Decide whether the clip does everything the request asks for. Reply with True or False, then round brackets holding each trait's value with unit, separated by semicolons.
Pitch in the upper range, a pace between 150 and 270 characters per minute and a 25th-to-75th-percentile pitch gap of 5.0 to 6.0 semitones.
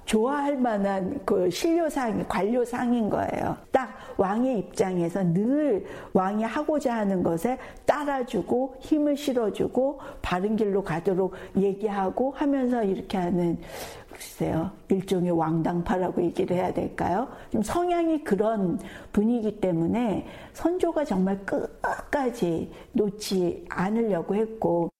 True (215 Hz; 260 characters per minute; 5.6 semitones)